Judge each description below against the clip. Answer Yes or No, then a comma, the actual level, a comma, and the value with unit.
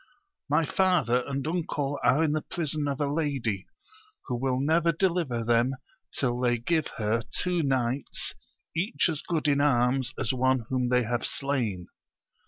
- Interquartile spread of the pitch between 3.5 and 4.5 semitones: Yes, average, 4.2 semitones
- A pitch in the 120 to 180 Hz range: Yes, low, 135 Hz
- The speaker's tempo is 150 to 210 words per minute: Yes, average, 165 wpm